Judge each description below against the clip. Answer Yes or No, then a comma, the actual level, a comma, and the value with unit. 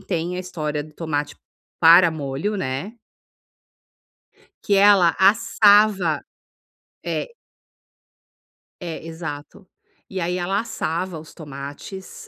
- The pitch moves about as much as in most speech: Yes, average, 3.9 semitones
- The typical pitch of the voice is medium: Yes, medium, 170 Hz